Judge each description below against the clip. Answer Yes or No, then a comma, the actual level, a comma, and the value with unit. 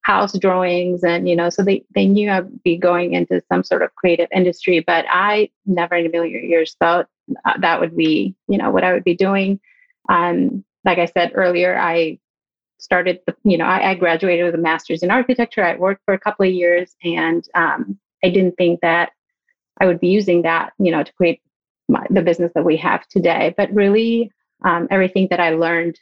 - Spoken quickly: Yes, fast, 210 wpm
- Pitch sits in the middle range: Yes, medium, 180 Hz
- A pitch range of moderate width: No, narrow, 2.3 semitones